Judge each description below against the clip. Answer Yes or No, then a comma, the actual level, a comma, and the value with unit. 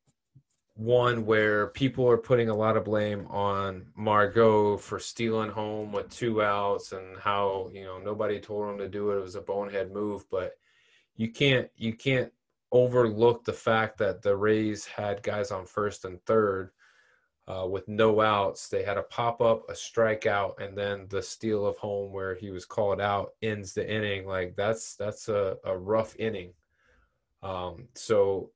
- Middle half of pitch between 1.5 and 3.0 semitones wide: Yes, narrow, 2.4 semitones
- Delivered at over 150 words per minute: Yes, average, 170 wpm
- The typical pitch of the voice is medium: No, low, 105 Hz